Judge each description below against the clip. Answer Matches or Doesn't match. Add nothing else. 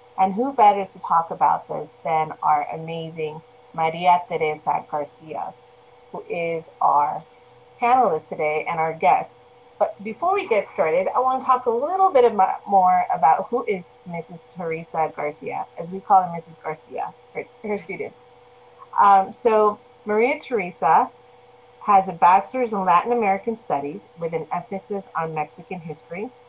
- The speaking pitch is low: Doesn't match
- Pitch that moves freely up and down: Matches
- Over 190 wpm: Doesn't match